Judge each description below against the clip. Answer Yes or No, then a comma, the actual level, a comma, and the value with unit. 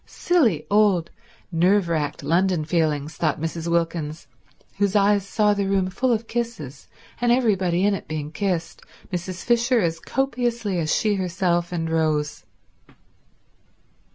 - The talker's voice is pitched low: No, medium, 180 Hz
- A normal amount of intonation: Yes, average, 4.2 semitones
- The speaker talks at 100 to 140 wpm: Yes, slow, 135 wpm